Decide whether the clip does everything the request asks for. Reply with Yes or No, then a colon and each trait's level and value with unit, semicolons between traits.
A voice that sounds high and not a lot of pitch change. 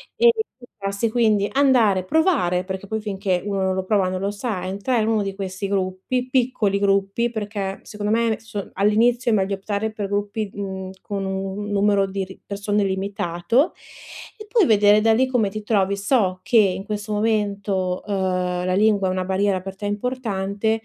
Yes: high, 200 Hz; narrow, 2.3 semitones